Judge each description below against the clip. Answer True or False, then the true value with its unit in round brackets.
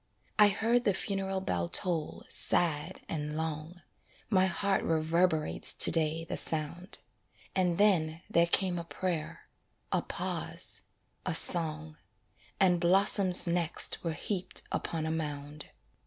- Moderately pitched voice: True (170 Hz)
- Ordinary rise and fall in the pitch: True (3.0 semitones)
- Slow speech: True (125 wpm)